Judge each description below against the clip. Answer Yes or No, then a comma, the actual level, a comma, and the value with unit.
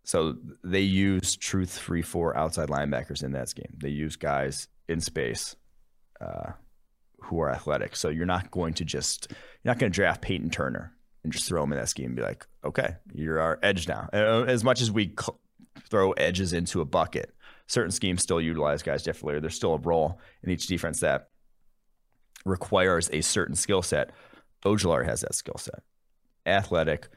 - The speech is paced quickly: No, average, 185 wpm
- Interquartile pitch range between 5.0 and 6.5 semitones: No, average, 3.8 semitones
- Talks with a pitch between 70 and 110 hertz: Yes, very low, 85 Hz